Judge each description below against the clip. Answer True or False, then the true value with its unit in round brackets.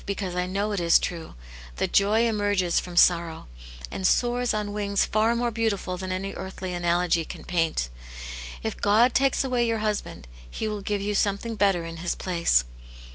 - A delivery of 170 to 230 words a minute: True (185 wpm)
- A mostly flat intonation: False (3.3 semitones)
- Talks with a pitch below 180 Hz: False (200 Hz)